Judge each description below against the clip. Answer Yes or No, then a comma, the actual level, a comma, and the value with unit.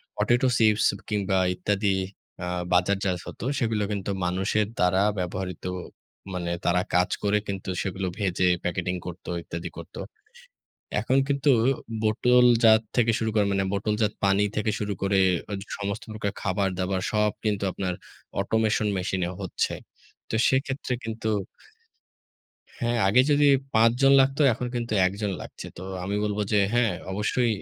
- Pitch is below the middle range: Yes, low, 105 Hz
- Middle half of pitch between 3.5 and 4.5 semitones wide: No, average, 2.9 semitones